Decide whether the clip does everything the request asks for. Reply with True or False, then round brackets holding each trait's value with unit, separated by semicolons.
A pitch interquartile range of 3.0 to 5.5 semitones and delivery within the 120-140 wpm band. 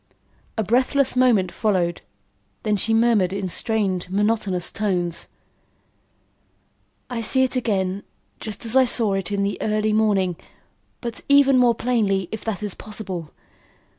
True (3.5 semitones; 135 wpm)